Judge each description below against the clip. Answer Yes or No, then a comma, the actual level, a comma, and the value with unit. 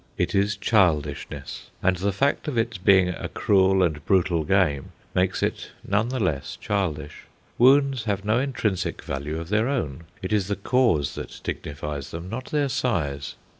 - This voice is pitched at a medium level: No, very low, 95 Hz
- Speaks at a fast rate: No, average, 170 wpm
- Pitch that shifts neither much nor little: No, wide, 6.1 semitones